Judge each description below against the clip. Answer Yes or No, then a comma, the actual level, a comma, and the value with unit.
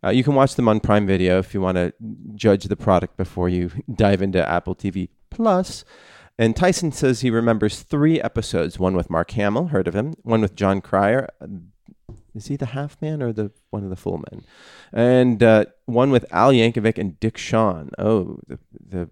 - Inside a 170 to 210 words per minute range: Yes, average, 200 wpm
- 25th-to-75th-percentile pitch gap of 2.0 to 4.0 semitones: No, average, 4.9 semitones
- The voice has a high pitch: No, low, 105 Hz